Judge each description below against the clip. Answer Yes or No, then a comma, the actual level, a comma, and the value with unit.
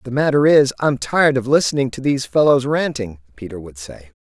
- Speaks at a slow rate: No, average, 200 wpm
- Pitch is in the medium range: No, low, 130 Hz